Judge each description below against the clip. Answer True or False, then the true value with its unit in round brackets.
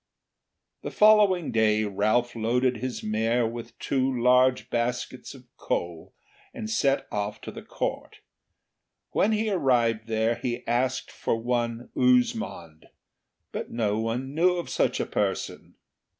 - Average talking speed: False (130 wpm)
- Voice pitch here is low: True (120 Hz)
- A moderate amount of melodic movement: True (3.2 semitones)